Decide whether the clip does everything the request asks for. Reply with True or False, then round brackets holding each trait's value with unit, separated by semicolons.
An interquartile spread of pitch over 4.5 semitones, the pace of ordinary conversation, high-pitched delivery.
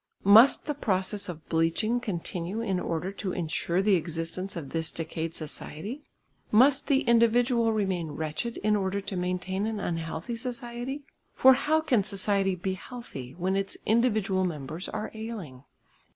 True (5.4 semitones; 150 wpm; 195 Hz)